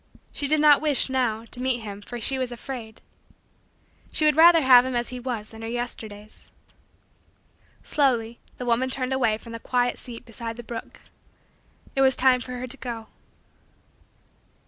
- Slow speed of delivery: No, average, 170 wpm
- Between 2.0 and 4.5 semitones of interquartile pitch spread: Yes, narrow, 2.4 semitones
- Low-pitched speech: No, high, 245 Hz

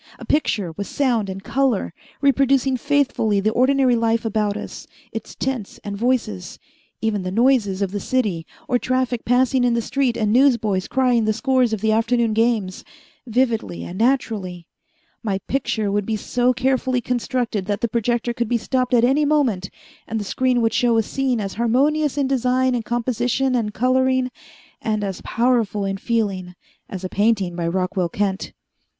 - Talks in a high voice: Yes, high, 235 Hz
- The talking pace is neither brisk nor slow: Yes, average, 170 wpm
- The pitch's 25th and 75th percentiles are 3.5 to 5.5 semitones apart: Yes, average, 3.8 semitones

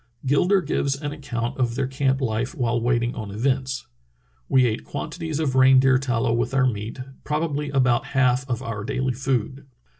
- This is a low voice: Yes, low, 130 Hz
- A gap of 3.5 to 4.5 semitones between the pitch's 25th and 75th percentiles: No, narrow, 2.5 semitones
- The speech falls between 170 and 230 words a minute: Yes, average, 175 wpm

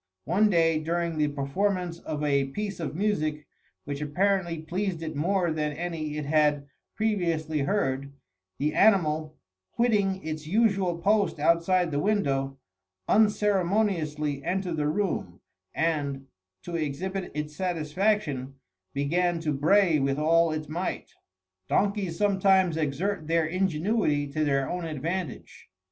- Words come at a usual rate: No, slow, 125 wpm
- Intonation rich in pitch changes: No, average, 4.1 semitones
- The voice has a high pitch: No, medium, 165 Hz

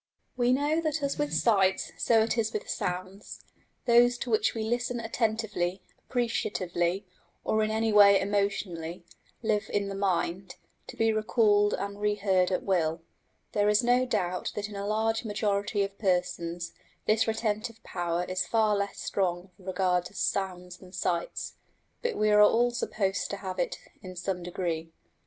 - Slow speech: No, average, 165 wpm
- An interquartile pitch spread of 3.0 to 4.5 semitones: Yes, average, 3.3 semitones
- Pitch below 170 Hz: No, high, 205 Hz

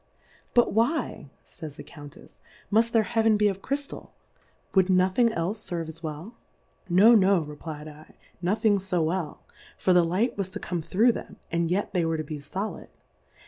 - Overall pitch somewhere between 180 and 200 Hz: Yes, medium, 185 Hz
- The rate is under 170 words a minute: No, average, 190 wpm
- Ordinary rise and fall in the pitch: Yes, average, 4.8 semitones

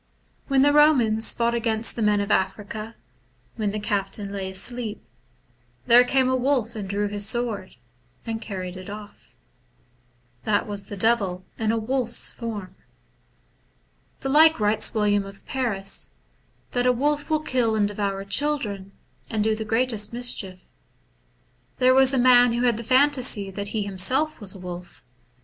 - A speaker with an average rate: Yes, average, 160 wpm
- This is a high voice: Yes, high, 220 Hz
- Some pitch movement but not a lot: Yes, average, 3.6 semitones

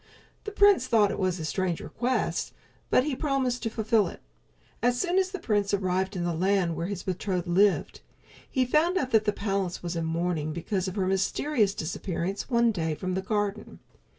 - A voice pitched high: Yes, high, 200 Hz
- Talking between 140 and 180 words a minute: No, average, 190 wpm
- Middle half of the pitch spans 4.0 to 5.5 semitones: Yes, average, 5.2 semitones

